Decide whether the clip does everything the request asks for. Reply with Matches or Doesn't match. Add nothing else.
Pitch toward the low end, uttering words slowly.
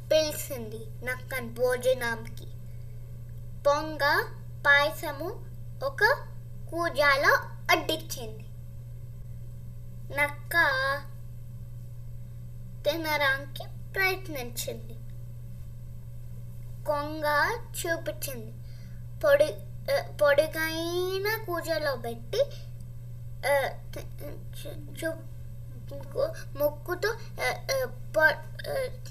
Matches